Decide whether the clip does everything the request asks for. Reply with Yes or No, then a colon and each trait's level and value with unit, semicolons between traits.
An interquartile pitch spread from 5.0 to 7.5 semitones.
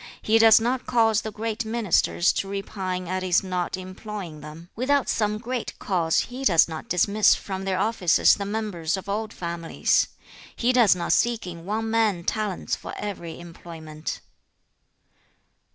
No: average, 4.2 semitones